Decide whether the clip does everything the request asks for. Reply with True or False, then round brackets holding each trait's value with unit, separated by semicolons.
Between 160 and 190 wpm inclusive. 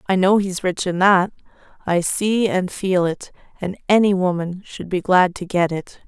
False (200 wpm)